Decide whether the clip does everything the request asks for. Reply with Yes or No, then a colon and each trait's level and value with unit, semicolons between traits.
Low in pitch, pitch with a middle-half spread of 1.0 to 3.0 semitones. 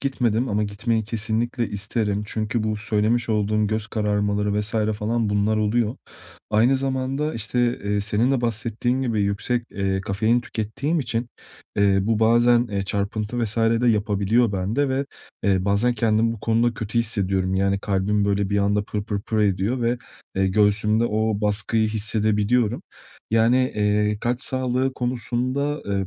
Yes: low, 110 Hz; narrow, 2.6 semitones